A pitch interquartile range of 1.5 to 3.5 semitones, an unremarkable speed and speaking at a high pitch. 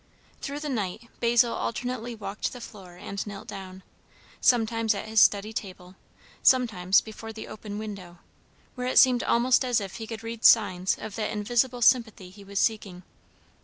Yes: average, 3.2 semitones; average, 165 wpm; high, 220 Hz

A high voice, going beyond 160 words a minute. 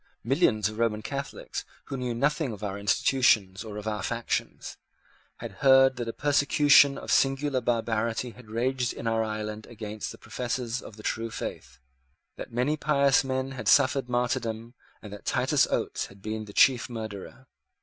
No: low, 120 Hz; average, 170 wpm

